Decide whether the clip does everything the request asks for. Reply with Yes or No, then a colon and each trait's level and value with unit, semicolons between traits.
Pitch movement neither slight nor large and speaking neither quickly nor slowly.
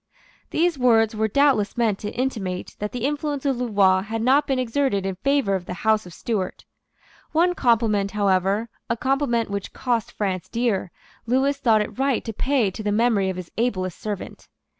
Yes: average, 4.7 semitones; average, 180 wpm